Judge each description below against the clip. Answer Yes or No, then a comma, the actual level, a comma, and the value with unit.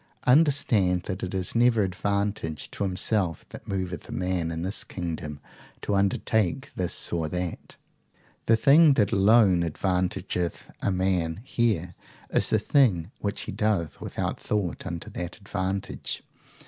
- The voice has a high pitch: No, very low, 95 Hz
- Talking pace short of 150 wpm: Yes, average, 140 wpm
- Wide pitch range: No, average, 3.2 semitones